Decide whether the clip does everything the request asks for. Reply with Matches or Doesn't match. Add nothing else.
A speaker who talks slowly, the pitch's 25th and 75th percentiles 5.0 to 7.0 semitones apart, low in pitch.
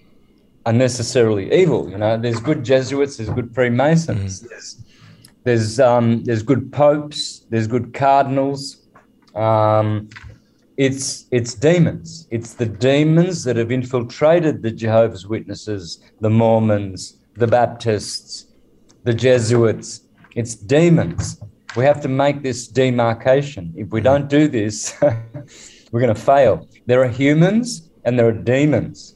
Doesn't match